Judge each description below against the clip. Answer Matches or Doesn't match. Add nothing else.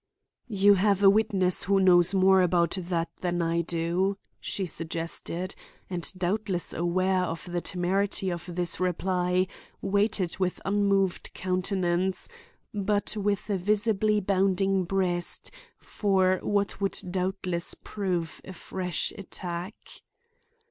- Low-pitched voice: Doesn't match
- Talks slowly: Matches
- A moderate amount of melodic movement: Doesn't match